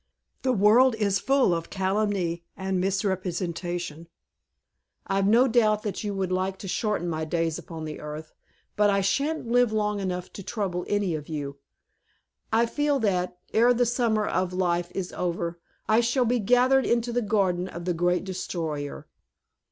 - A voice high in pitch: Yes, high, 195 Hz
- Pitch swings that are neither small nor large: Yes, average, 4.2 semitones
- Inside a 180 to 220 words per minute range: No, average, 160 wpm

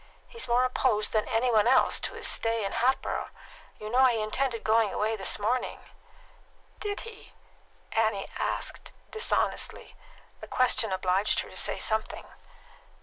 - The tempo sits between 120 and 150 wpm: Yes, average, 145 wpm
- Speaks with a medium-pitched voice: No, high, 225 Hz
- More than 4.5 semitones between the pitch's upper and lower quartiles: No, average, 3.0 semitones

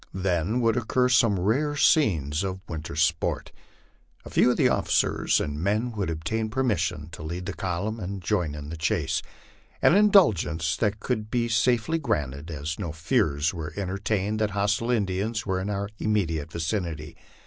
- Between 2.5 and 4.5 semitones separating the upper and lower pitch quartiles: No, average, 5.3 semitones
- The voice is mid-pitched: No, low, 100 Hz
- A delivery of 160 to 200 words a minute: Yes, average, 170 wpm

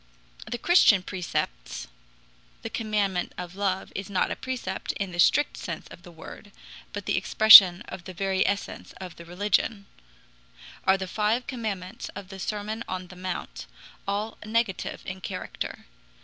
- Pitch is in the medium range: No, high, 195 Hz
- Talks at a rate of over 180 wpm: No, average, 155 wpm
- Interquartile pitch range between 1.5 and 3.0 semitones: Yes, narrow, 2.5 semitones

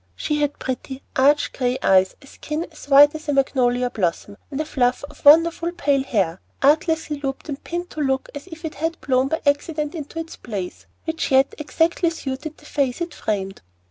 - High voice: Yes, very high, 285 Hz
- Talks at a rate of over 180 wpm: Yes, average, 195 wpm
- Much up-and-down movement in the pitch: No, average, 3.2 semitones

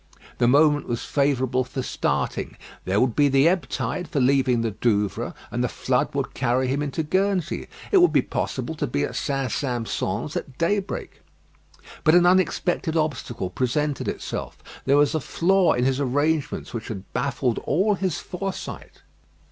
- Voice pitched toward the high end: No, medium, 140 Hz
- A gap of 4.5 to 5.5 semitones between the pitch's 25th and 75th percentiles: Yes, average, 4.8 semitones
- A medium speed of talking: Yes, average, 165 wpm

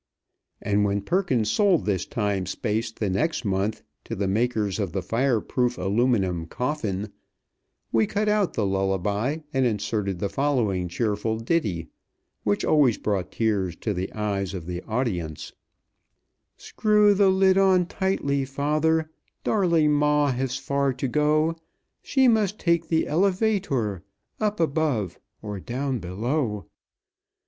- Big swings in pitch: Yes, wide, 7.6 semitones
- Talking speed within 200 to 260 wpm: No, slow, 135 wpm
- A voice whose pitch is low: Yes, low, 120 Hz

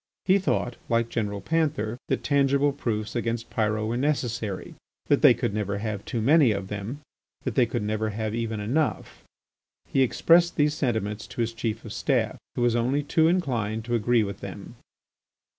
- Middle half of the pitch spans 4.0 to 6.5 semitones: Yes, average, 4.5 semitones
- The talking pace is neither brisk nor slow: Yes, average, 175 wpm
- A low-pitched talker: Yes, low, 115 Hz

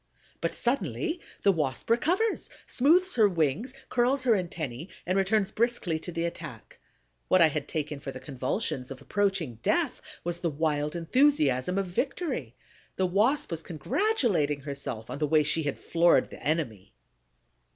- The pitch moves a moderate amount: No, wide, 7.7 semitones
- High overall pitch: No, medium, 170 Hz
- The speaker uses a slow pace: No, average, 155 wpm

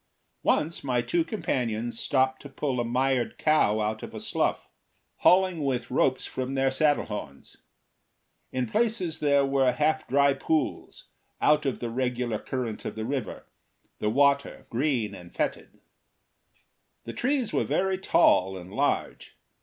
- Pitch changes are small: No, average, 4.1 semitones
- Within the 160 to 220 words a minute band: No, average, 145 wpm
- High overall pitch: No, low, 130 Hz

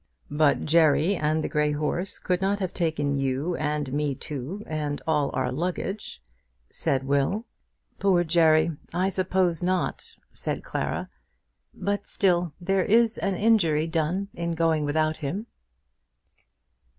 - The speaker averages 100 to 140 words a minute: Yes, slow, 135 wpm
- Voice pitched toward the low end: No, medium, 165 Hz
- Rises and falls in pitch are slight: No, average, 3.9 semitones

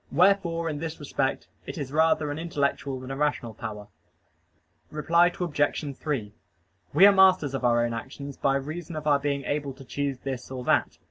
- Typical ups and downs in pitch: Yes, average, 3.3 semitones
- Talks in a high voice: No, medium, 145 Hz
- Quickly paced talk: No, average, 185 wpm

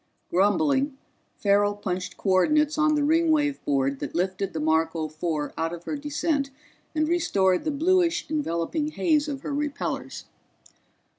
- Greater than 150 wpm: No, average, 140 wpm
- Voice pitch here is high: Yes, very high, 275 Hz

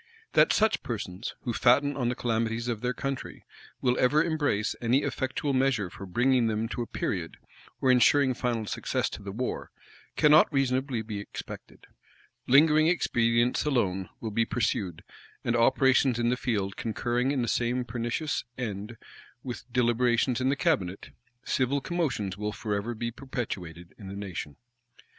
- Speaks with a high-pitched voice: No, low, 120 Hz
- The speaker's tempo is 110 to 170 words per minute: Yes, average, 155 wpm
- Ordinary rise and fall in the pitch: Yes, average, 3.3 semitones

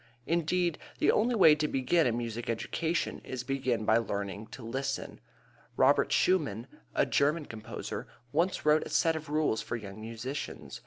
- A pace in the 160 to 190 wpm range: Yes, average, 165 wpm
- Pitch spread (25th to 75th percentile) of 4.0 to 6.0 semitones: Yes, wide, 5.6 semitones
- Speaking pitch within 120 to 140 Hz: Yes, low, 135 Hz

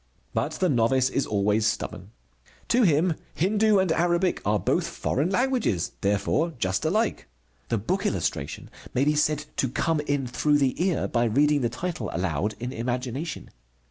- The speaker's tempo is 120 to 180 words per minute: Yes, average, 160 wpm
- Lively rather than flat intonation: Yes, wide, 7.1 semitones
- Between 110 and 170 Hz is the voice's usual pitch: Yes, medium, 140 Hz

